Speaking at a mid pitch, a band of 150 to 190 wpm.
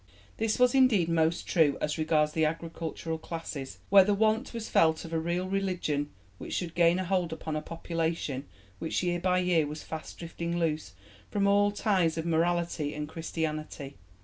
Yes: medium, 165 Hz; average, 175 wpm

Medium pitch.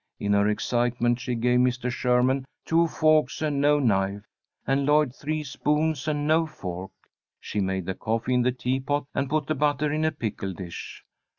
No: low, 130 Hz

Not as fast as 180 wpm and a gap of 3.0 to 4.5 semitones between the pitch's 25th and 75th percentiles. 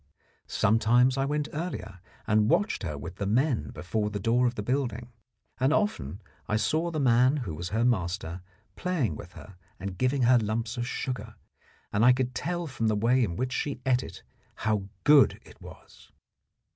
No: average, 185 wpm; average, 4.2 semitones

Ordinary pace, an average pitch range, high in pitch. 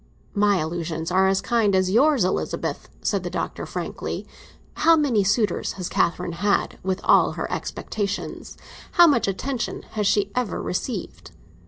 Yes: average, 145 wpm; average, 4.0 semitones; high, 200 Hz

